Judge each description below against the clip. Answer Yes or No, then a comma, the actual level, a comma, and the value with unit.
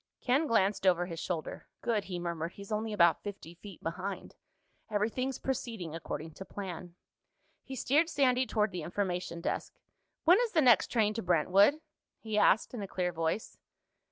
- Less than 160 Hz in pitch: No, high, 200 Hz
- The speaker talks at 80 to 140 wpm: No, average, 165 wpm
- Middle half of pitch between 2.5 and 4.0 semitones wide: No, average, 4.9 semitones